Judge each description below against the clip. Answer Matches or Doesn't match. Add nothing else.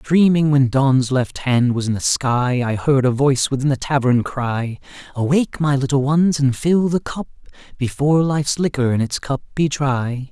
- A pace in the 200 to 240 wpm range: Doesn't match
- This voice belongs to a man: Matches